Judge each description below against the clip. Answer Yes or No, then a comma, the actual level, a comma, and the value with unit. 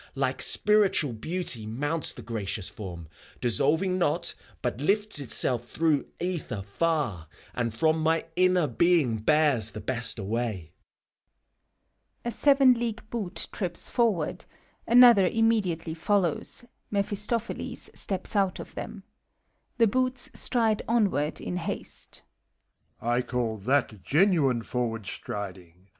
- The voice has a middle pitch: Yes, medium, 160 Hz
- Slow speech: Yes, slow, 120 wpm